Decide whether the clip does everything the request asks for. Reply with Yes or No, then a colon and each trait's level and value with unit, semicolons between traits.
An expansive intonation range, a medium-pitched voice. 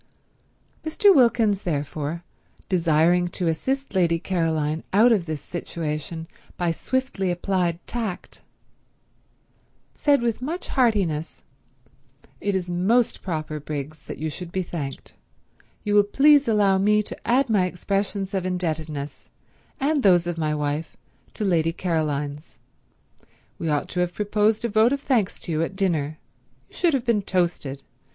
No: average, 4.9 semitones; medium, 180 Hz